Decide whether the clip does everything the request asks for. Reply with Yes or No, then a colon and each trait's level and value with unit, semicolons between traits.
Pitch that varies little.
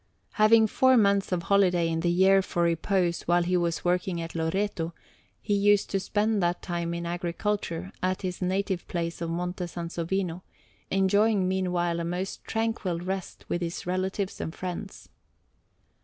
Yes: narrow, 2.2 semitones